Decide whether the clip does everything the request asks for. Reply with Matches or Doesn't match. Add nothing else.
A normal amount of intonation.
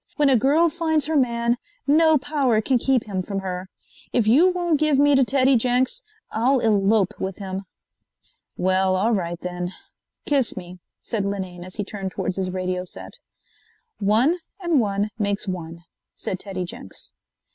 Doesn't match